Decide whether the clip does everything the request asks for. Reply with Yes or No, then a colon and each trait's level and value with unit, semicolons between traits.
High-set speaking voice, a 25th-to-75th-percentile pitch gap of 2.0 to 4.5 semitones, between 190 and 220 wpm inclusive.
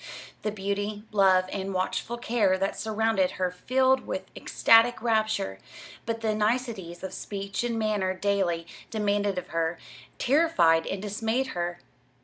No: high, 205 Hz; average, 3.3 semitones; average, 140 wpm